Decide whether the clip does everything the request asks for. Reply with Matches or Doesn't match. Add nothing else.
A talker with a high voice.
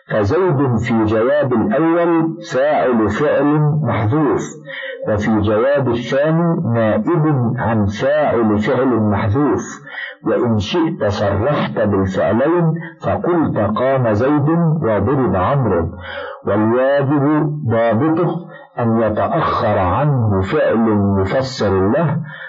Doesn't match